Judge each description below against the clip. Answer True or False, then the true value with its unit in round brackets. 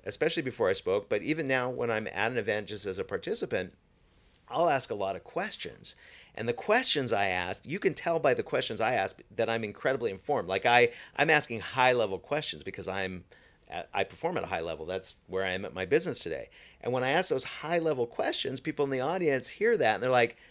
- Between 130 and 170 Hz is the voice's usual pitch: True (135 Hz)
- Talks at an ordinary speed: False (230 wpm)